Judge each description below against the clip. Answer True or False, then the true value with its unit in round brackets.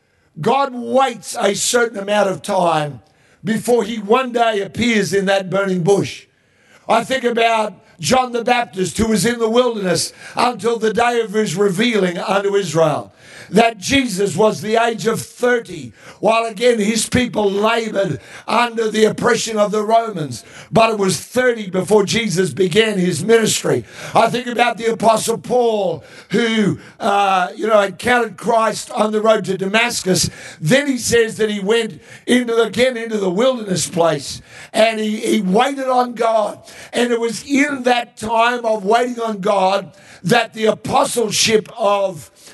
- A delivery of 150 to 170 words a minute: True (160 wpm)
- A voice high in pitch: True (220 Hz)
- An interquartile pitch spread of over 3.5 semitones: False (3.2 semitones)